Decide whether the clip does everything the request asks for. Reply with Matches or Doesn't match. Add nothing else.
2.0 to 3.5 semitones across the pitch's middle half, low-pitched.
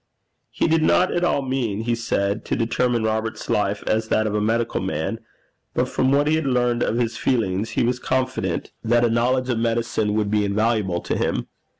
Matches